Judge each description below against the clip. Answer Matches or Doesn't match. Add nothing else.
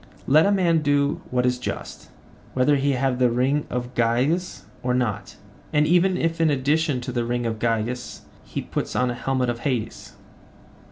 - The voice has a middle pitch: Doesn't match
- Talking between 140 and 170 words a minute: Doesn't match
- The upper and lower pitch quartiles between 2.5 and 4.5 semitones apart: Matches